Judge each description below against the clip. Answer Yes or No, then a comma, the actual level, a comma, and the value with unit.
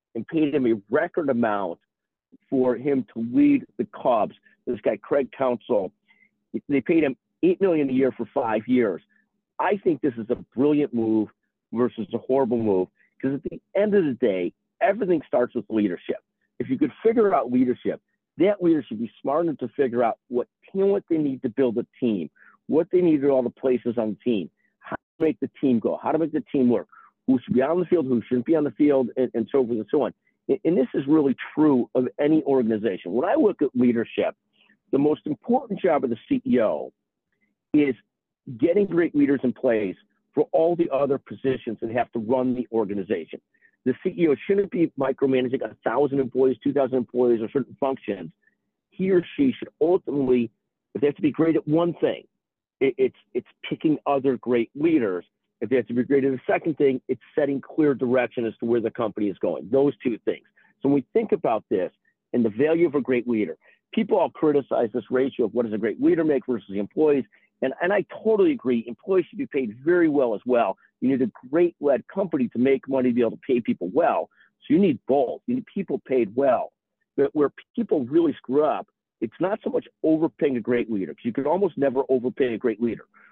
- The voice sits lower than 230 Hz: Yes, low, 135 Hz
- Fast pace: Yes, fast, 215 wpm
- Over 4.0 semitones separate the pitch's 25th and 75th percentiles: Yes, average, 5.2 semitones